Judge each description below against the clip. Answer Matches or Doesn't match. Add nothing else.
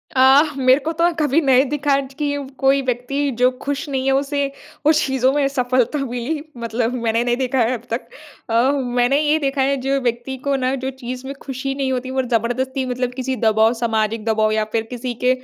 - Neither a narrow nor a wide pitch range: Doesn't match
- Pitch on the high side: Matches